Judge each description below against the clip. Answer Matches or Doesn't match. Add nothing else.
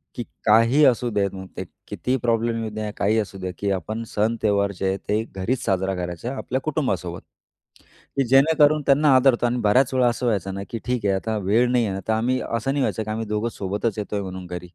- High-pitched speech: Doesn't match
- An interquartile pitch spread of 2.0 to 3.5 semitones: Doesn't match